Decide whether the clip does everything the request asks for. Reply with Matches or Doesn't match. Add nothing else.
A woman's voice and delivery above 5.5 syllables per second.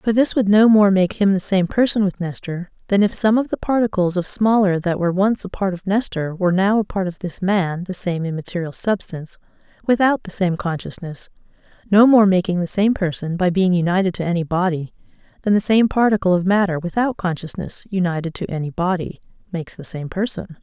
Matches